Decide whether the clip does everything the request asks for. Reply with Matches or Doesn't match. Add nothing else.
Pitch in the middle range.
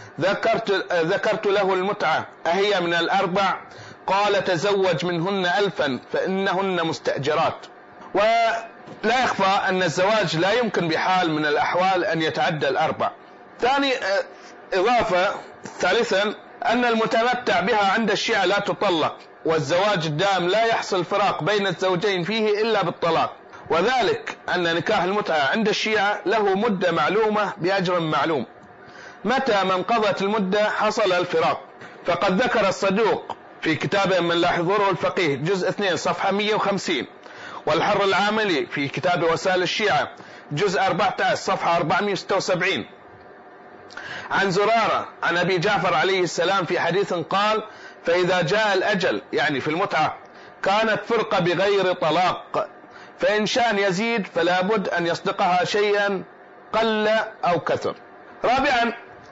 Doesn't match